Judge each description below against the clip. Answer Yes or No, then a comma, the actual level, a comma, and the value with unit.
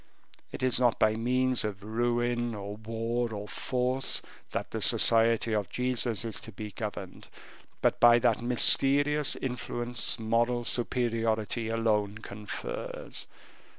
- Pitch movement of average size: No, narrow, 1.9 semitones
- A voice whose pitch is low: Yes, low, 115 Hz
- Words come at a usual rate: No, slow, 125 wpm